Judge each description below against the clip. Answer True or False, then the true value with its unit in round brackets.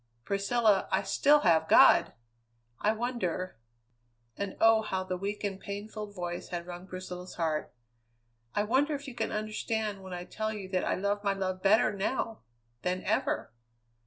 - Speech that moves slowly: False (160 wpm)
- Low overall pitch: False (200 Hz)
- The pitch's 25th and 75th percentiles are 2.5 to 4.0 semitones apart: True (2.8 semitones)